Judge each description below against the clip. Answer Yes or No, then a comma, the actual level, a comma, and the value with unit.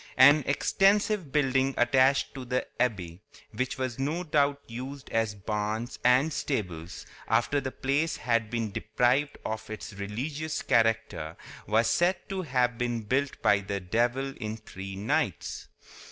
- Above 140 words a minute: No, slow, 135 wpm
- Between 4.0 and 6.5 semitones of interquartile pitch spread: Yes, average, 4.4 semitones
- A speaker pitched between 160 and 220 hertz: No, low, 125 Hz